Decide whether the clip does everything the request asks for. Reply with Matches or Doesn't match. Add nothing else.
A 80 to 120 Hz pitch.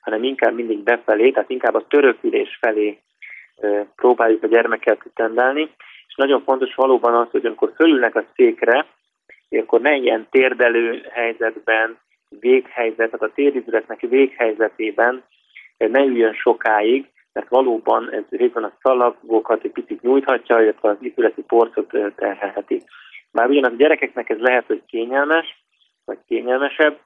Doesn't match